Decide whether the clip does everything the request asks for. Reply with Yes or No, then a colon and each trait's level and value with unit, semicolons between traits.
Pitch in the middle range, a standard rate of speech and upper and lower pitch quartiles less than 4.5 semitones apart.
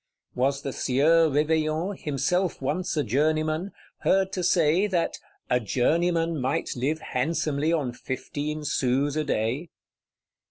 No: medium, 155 Hz; slow, 125 wpm; average, 3.5 semitones